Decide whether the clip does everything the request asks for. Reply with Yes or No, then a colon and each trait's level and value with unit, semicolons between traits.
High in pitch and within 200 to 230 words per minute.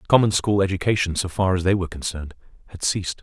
No: very low, 95 Hz; fast, 205 wpm